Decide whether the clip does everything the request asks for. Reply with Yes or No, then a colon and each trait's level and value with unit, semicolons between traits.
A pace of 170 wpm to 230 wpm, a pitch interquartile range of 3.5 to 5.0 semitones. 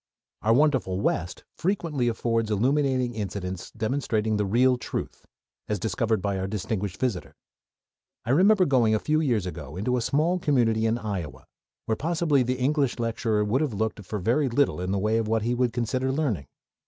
Yes: average, 180 wpm; average, 4.0 semitones